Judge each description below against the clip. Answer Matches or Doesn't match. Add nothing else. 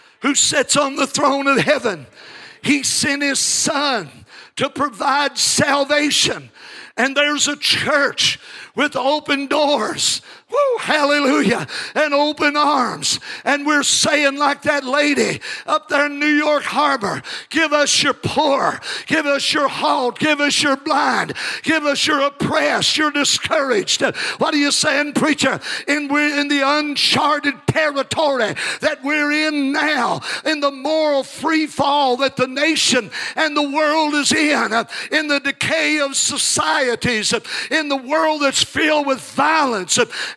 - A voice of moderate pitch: Doesn't match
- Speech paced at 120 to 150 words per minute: Matches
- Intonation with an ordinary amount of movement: Doesn't match